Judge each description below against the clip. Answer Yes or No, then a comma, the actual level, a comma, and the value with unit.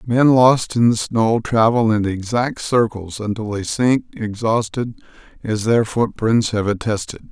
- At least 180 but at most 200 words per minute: No, average, 150 wpm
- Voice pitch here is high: No, low, 115 Hz